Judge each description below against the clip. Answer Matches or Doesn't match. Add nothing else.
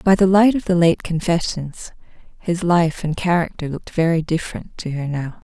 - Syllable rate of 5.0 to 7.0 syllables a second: Matches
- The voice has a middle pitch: Matches